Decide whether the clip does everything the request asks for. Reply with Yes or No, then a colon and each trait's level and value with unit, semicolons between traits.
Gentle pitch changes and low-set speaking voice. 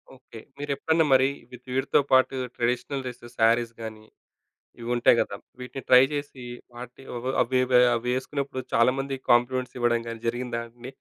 Yes: narrow, 1.9 semitones; low, 125 Hz